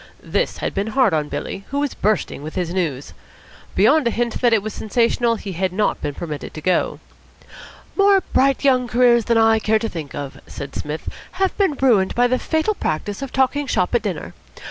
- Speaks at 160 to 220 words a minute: Yes, fast, 205 wpm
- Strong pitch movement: Yes, wide, 6.0 semitones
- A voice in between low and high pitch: No, high, 225 Hz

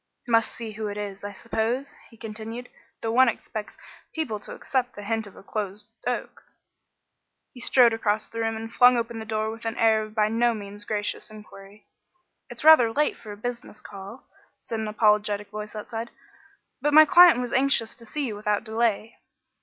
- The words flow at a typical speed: Yes, average, 190 wpm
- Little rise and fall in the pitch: Yes, narrow, 2.0 semitones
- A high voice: Yes, high, 225 Hz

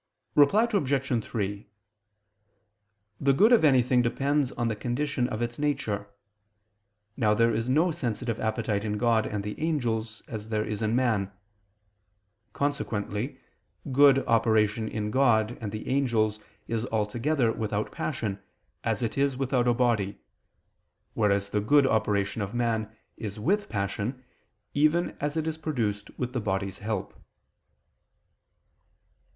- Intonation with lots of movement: No, average, 4.3 semitones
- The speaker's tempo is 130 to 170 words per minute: Yes, slow, 135 wpm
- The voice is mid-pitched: No, low, 115 Hz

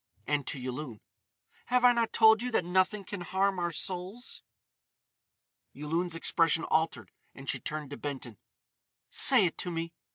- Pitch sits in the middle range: Yes, medium, 170 Hz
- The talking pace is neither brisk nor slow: Yes, average, 155 wpm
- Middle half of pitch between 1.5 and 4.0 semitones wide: No, average, 4.8 semitones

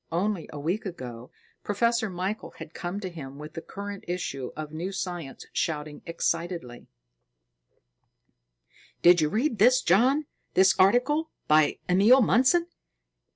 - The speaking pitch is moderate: Yes, medium, 180 Hz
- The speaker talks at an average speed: No, slow, 130 wpm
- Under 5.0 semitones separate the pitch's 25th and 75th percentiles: No, wide, 5.5 semitones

